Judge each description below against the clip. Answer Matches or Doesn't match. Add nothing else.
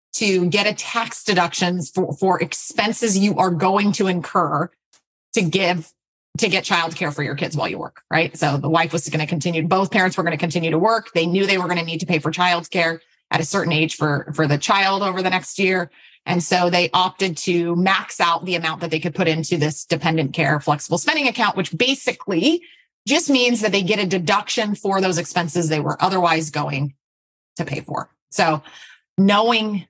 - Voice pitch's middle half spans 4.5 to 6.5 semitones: Doesn't match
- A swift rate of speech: Matches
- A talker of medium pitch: Matches